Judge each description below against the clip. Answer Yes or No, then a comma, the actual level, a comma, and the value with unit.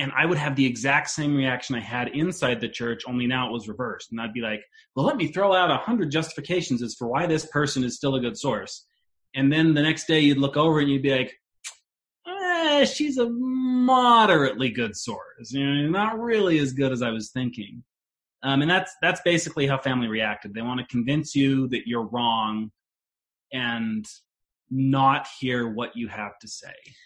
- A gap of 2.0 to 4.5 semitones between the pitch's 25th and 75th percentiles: No, average, 5.1 semitones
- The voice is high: No, low, 135 Hz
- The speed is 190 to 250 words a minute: Yes, average, 200 wpm